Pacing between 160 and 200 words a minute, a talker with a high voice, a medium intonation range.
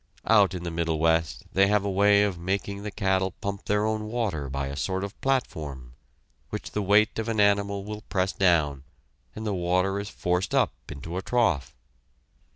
No: average, 190 wpm; very low, 95 Hz; average, 3.4 semitones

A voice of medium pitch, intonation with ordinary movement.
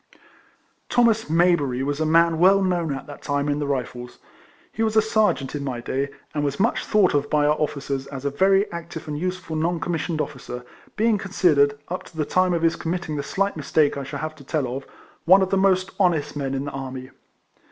Yes: medium, 155 Hz; average, 4.6 semitones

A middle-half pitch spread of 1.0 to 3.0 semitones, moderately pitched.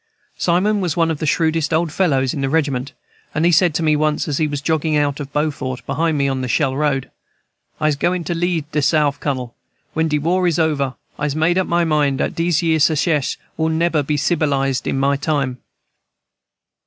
Yes: average, 2.7 semitones; medium, 150 Hz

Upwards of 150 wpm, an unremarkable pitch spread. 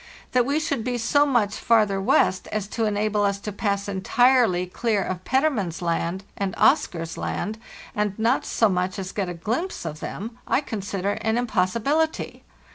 Yes: average, 180 wpm; average, 4.1 semitones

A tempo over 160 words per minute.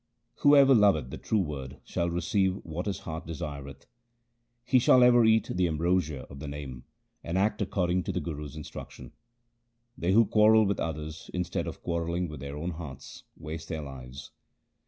Yes: average, 170 wpm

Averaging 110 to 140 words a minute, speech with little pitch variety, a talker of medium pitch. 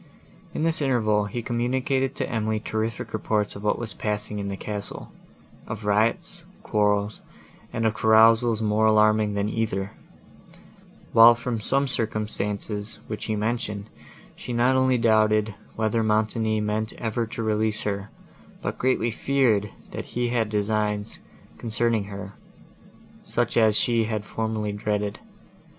No: slow, 135 wpm; narrow, 1.7 semitones; low, 110 Hz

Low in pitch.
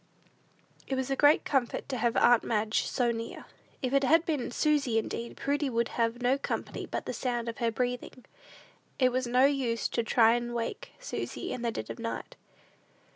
No: high, 245 Hz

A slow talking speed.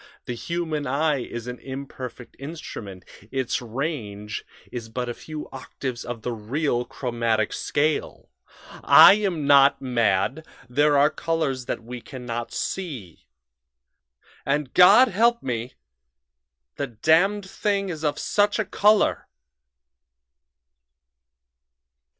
Yes: slow, 115 wpm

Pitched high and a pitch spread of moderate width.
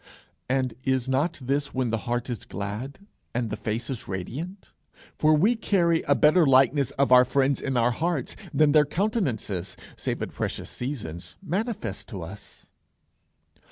No: low, 135 Hz; average, 4.6 semitones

